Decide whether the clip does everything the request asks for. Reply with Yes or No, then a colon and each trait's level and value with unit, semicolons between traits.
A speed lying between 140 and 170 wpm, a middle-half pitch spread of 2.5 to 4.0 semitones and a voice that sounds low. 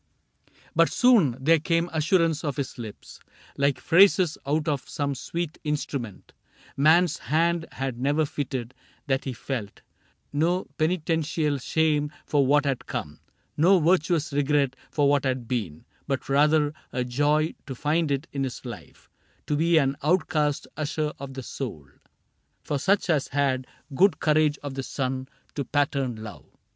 No: average, 160 wpm; average, 2.9 semitones; medium, 145 Hz